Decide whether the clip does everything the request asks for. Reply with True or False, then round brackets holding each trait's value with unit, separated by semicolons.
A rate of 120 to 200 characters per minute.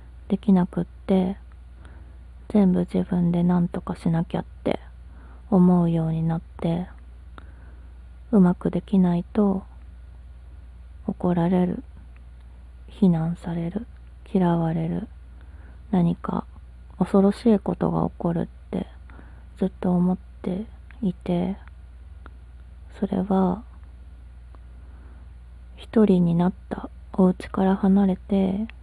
True (180 characters per minute)